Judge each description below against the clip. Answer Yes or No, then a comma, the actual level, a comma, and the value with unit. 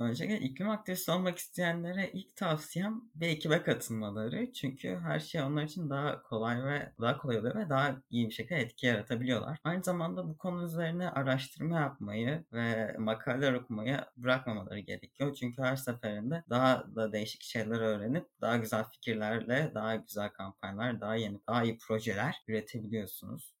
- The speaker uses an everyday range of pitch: No, wide, 6.1 semitones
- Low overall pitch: Yes, low, 130 Hz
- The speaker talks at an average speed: No, fast, 155 wpm